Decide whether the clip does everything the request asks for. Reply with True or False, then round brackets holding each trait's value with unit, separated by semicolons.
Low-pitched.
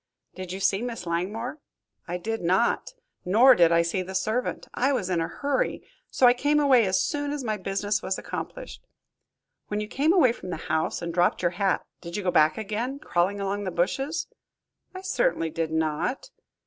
False (200 Hz)